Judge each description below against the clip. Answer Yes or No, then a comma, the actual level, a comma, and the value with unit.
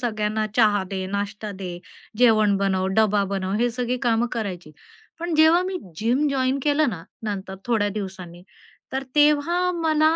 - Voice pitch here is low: No, high, 220 Hz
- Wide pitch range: Yes, wide, 5.8 semitones